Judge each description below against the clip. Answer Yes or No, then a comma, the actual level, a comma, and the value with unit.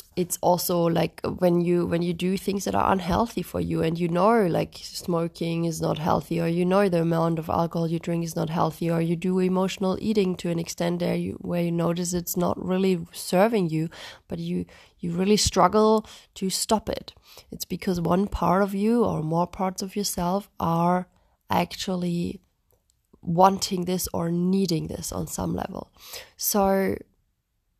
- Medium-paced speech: Yes, average, 175 wpm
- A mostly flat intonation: Yes, narrow, 2.2 semitones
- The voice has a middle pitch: Yes, medium, 175 Hz